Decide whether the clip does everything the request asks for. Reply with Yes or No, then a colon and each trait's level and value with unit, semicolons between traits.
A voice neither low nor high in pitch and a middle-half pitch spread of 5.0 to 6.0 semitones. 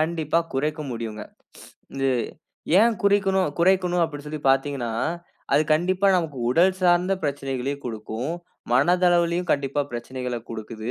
Yes: medium, 150 Hz; average, 5.3 semitones